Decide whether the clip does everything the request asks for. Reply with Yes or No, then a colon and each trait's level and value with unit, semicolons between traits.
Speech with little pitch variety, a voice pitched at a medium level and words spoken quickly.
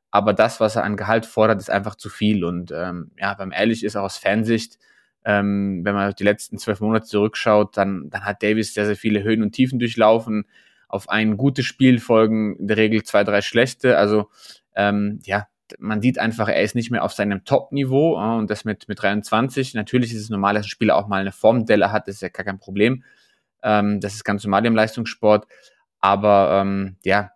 No: narrow, 1.8 semitones; low, 105 Hz; fast, 215 wpm